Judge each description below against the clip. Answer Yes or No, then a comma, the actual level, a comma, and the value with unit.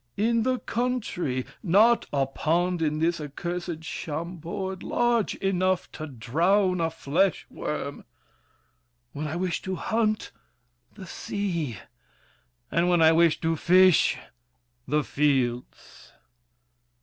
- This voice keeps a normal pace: No, slow, 110 wpm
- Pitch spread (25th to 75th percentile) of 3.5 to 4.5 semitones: Yes, average, 4.1 semitones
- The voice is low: No, medium, 170 Hz